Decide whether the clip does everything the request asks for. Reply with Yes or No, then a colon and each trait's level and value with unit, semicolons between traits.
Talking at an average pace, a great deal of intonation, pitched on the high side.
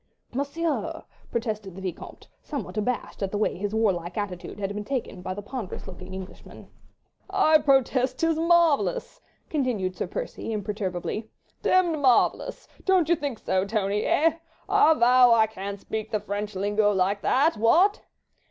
Yes: average, 150 wpm; wide, 6.2 semitones; high, 220 Hz